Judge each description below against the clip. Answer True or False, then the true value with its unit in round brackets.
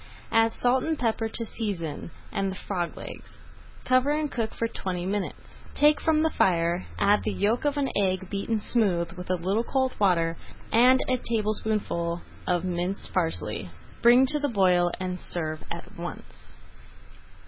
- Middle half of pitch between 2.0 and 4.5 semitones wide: False (5.3 semitones)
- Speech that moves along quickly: False (160 wpm)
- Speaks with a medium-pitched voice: False (205 Hz)